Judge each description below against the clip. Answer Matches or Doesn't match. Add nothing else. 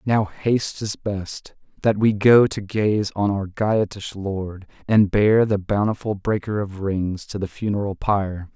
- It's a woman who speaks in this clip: Doesn't match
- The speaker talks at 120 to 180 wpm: Matches